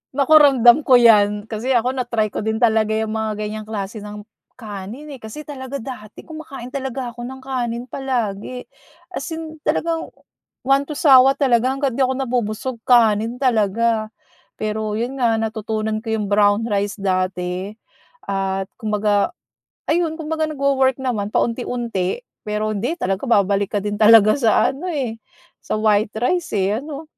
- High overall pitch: Yes, high, 230 Hz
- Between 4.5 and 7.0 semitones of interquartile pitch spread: No, average, 4.0 semitones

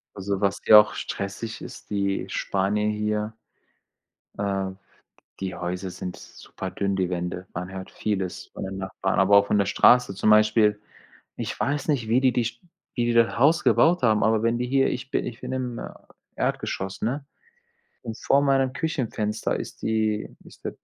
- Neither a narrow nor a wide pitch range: Yes, average, 3.7 semitones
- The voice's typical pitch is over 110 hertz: No, low, 105 Hz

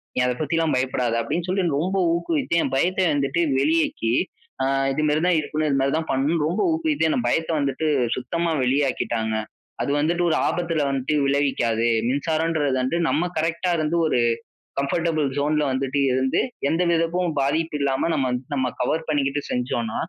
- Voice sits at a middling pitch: Yes, medium, 150 Hz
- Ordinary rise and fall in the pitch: Yes, average, 3.6 semitones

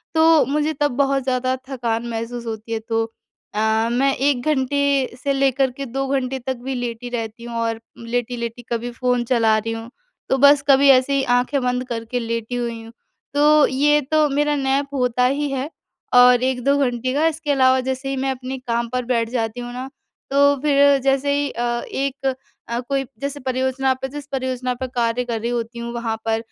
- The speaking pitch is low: No, very high, 255 Hz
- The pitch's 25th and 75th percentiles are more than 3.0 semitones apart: No, average, 2.7 semitones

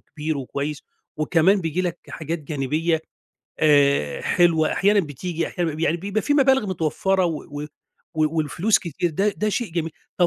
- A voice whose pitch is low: No, medium, 165 Hz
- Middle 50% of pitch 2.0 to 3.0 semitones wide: No, average, 3.6 semitones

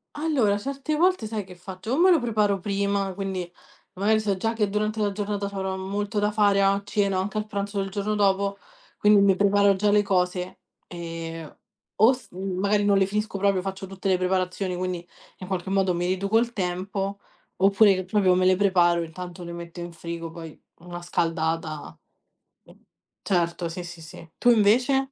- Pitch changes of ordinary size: No, narrow, 2.3 semitones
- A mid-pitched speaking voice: No, high, 195 Hz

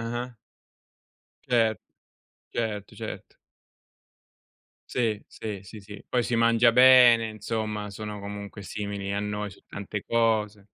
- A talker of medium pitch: No, low, 110 Hz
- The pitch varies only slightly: Yes, narrow, 2.2 semitones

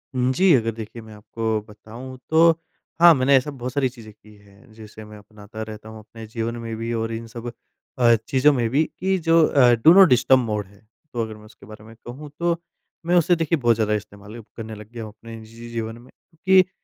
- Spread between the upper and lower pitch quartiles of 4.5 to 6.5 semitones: No, average, 3.4 semitones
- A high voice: No, low, 115 Hz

